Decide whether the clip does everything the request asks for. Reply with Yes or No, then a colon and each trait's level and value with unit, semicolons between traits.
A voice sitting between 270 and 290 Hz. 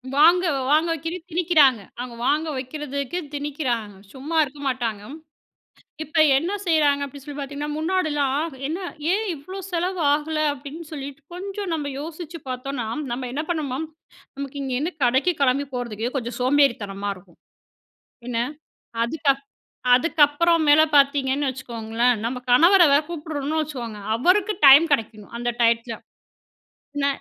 Yes: very high, 285 Hz